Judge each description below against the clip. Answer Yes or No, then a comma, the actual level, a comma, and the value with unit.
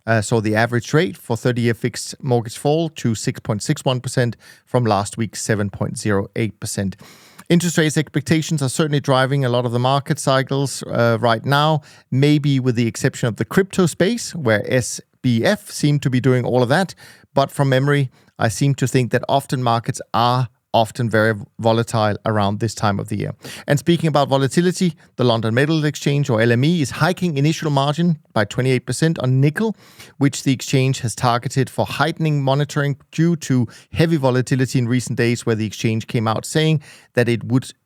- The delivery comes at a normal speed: Yes, average, 175 wpm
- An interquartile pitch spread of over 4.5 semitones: No, average, 3.9 semitones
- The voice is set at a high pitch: No, low, 130 Hz